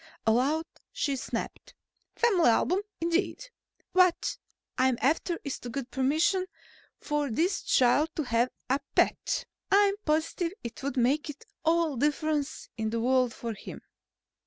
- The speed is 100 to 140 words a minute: Yes, slow, 135 wpm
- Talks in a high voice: Yes, very high, 295 Hz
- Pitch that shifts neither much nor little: Yes, average, 4.8 semitones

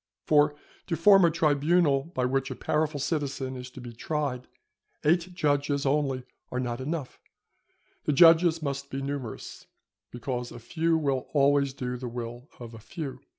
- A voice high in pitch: No, medium, 140 Hz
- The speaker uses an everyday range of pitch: Yes, average, 3.4 semitones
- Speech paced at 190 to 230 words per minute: No, average, 160 wpm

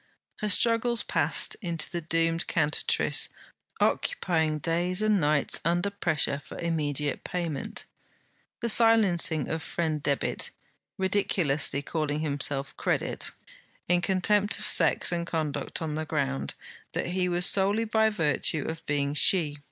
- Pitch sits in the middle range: Yes, medium, 165 Hz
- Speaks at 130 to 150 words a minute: Yes, slow, 135 wpm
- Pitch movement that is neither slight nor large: Yes, average, 4.0 semitones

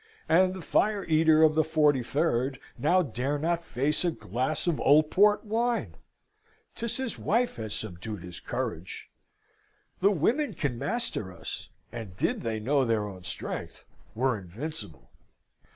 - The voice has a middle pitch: Yes, medium, 150 Hz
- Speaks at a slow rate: No, average, 145 wpm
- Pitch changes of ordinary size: No, wide, 7.7 semitones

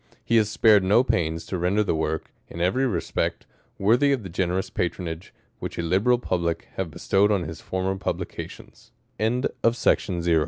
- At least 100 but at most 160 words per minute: Yes, average, 150 wpm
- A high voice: No, very low, 95 Hz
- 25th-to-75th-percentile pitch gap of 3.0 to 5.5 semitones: Yes, average, 3.9 semitones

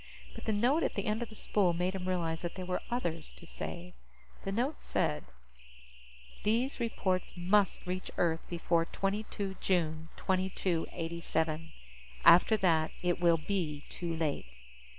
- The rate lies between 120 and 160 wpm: Yes, average, 150 wpm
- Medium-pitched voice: Yes, medium, 180 Hz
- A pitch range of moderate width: Yes, average, 3.3 semitones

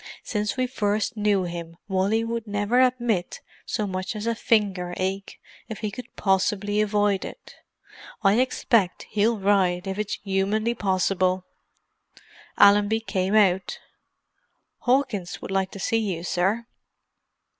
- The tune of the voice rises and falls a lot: No, narrow, 2.6 semitones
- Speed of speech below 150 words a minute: Yes, slow, 135 wpm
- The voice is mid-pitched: No, high, 205 Hz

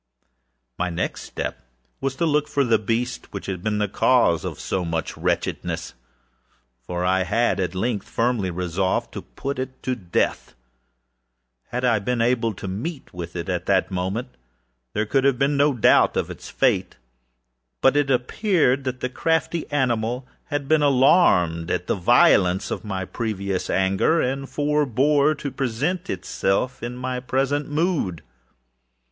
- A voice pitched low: Yes, low, 120 Hz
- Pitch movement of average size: No, wide, 6.6 semitones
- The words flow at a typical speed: Yes, average, 160 wpm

